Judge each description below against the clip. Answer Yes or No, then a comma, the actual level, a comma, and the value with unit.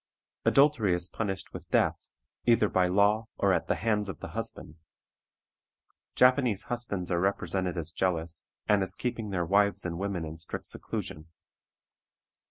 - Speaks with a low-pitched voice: Yes, very low, 95 Hz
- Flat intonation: No, average, 3.4 semitones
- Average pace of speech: Yes, average, 150 wpm